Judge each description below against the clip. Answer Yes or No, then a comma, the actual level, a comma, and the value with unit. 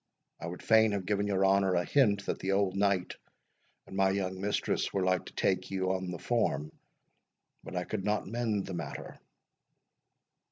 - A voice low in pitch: Yes, very low, 95 Hz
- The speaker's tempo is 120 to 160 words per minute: No, average, 185 wpm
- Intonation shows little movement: Yes, narrow, 1.7 semitones